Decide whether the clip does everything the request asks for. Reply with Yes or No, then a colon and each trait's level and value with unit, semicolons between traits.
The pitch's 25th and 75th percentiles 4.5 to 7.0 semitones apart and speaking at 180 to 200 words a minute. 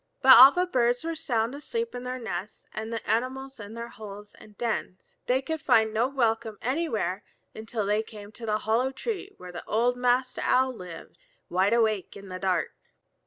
No: average, 3.5 semitones; average, 185 wpm